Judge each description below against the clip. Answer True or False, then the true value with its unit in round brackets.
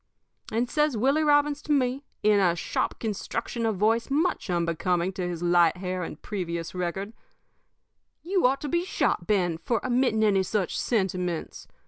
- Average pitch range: False (6.3 semitones)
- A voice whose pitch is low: False (210 Hz)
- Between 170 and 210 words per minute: False (160 wpm)